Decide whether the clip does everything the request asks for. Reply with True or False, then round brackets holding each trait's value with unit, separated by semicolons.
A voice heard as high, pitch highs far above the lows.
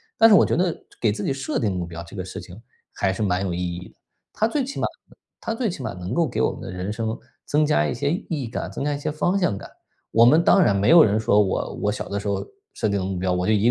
False (110 Hz; 8.1 semitones)